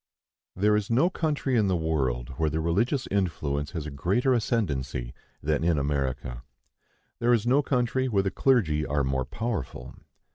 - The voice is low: Yes, very low, 85 Hz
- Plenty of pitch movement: Yes, wide, 8.9 semitones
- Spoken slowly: No, average, 160 wpm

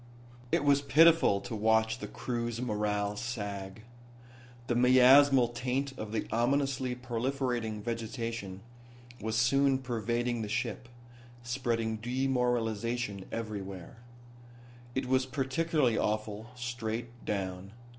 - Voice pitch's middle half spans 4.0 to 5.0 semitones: No, average, 2.8 semitones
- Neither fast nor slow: No, slow, 105 wpm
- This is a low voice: Yes, low, 120 Hz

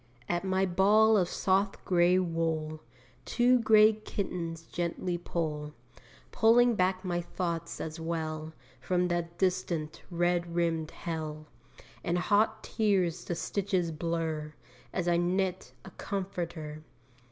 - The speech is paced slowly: Yes, slow, 120 wpm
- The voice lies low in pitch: No, medium, 175 Hz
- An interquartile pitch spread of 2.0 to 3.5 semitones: Yes, narrow, 2.5 semitones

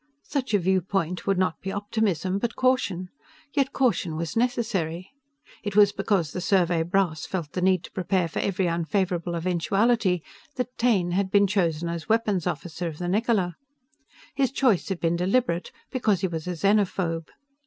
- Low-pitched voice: No, medium, 185 Hz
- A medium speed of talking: Yes, average, 165 wpm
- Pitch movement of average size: Yes, average, 3.4 semitones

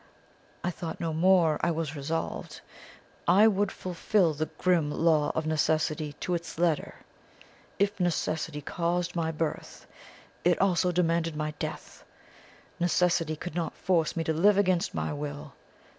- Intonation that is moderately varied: No, narrow, 2.2 semitones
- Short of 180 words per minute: Yes, average, 145 wpm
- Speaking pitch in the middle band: Yes, medium, 165 Hz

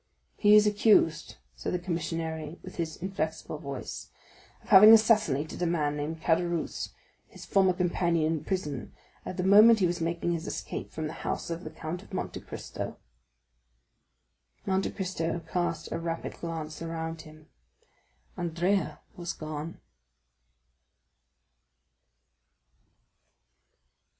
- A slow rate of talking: Yes, slow, 125 wpm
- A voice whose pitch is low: No, medium, 165 Hz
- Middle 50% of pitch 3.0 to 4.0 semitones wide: No, narrow, 2.6 semitones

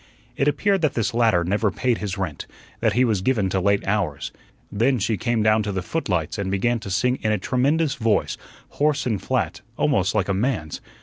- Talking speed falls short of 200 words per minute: No, fast, 205 wpm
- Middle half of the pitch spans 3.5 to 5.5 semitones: Yes, average, 4.4 semitones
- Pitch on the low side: Yes, low, 110 Hz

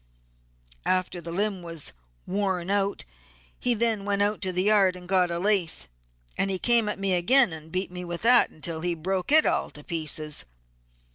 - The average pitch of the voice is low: No, medium, 185 Hz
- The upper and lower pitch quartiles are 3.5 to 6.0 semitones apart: No, average, 3.0 semitones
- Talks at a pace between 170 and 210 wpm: Yes, average, 190 wpm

